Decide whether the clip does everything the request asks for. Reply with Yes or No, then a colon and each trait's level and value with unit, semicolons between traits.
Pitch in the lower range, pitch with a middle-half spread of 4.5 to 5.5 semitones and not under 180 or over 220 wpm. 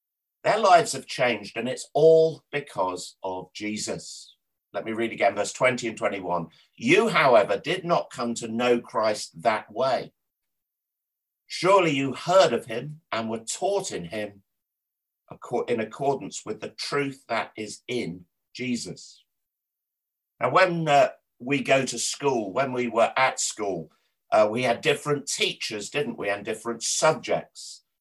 No: low, 120 Hz; average, 5.2 semitones; average, 150 wpm